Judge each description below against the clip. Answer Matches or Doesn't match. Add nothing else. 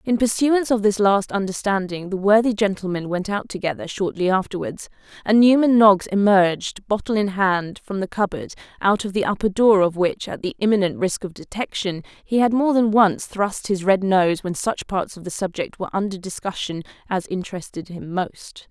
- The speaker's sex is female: Matches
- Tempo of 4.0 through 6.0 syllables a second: Matches